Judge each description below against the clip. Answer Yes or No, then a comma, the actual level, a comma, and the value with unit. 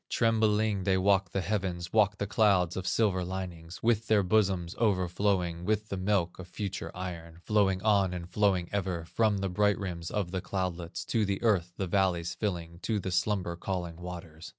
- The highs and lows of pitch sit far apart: No, average, 2.7 semitones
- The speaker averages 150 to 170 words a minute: No, average, 180 wpm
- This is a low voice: Yes, very low, 95 Hz